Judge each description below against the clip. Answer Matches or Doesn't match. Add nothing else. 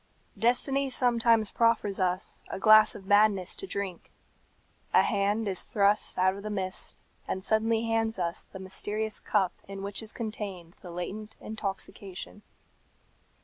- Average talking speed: Matches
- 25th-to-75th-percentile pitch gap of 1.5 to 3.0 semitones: Matches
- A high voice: Matches